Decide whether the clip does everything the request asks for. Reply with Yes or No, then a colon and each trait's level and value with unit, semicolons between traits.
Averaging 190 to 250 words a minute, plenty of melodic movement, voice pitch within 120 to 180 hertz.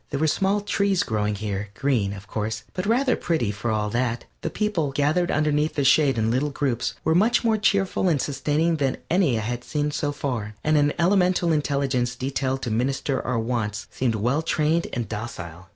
Yes: average, 200 wpm; wide, 5.7 semitones; medium, 140 Hz